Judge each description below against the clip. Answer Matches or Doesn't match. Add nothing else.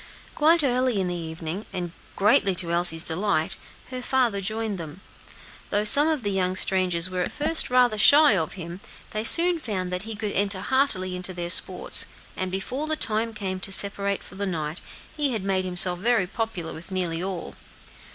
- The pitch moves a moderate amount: Matches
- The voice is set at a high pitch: Matches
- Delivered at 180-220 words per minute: Matches